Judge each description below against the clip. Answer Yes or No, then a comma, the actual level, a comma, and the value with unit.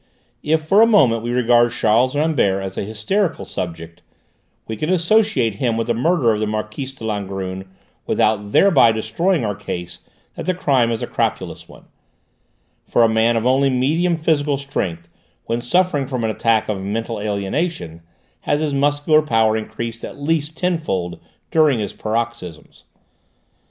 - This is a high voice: No, low, 120 Hz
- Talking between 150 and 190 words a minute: Yes, average, 160 wpm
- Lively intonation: Yes, wide, 5.9 semitones